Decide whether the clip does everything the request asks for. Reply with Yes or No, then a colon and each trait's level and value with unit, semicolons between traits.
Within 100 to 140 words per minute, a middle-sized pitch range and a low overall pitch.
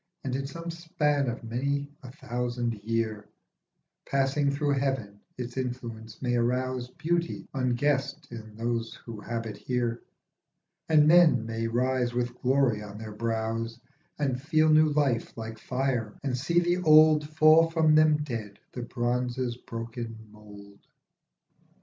Yes: slow, 135 wpm; average, 4.0 semitones; low, 125 Hz